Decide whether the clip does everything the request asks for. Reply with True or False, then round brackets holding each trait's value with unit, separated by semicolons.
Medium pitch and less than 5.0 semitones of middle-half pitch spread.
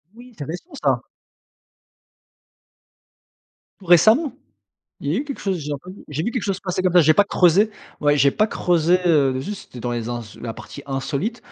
False (175 Hz; 6.4 semitones)